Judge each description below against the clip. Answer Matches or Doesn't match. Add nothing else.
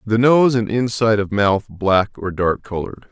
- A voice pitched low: Matches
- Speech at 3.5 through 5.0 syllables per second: Matches